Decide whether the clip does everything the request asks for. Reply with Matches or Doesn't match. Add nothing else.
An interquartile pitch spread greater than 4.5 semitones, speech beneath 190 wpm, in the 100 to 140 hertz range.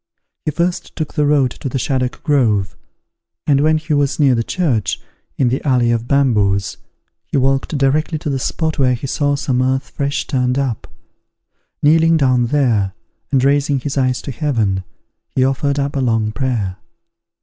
Doesn't match